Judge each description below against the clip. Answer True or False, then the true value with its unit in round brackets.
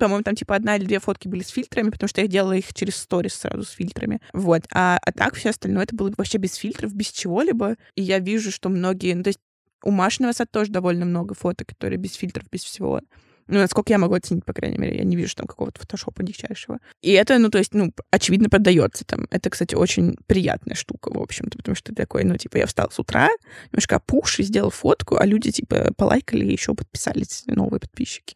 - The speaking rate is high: True (225 wpm)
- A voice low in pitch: False (195 Hz)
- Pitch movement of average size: False (2.2 semitones)